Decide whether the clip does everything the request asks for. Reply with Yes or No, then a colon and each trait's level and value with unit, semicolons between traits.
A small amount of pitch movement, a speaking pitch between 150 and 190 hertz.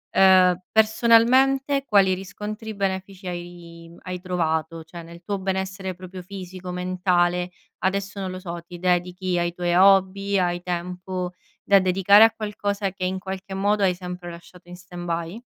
Yes: narrow, 1.9 semitones; medium, 185 Hz